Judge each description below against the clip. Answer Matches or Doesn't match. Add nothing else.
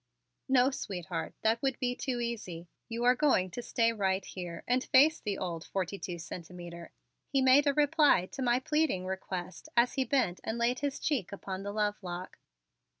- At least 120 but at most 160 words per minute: Doesn't match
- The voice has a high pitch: Matches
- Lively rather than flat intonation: Matches